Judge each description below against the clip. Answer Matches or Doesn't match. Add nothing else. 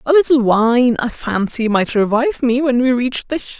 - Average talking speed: Doesn't match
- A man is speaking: Doesn't match